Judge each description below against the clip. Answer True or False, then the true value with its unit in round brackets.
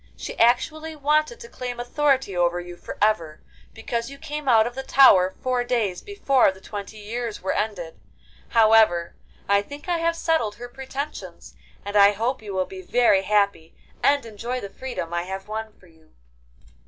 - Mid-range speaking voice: False (225 Hz)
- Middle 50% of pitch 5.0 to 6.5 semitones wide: True (5.5 semitones)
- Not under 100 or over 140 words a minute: False (180 wpm)